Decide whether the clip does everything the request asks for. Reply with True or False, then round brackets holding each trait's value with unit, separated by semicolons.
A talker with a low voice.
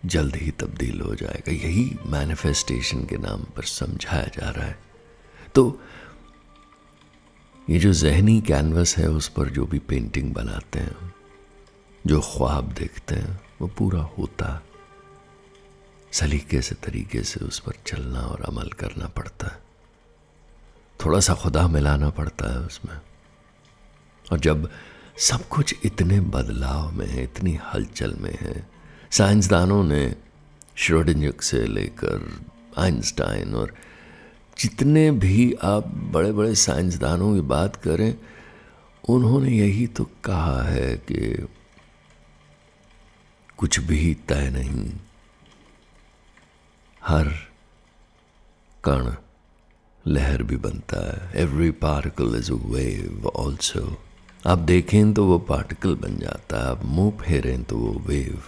True (80 Hz)